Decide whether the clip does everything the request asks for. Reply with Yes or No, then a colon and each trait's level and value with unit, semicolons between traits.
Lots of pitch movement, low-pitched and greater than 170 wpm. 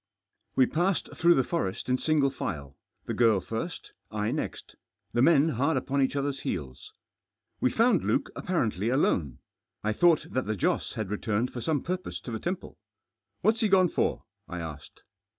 Yes: wide, 7.6 semitones; low, 130 Hz; average, 180 wpm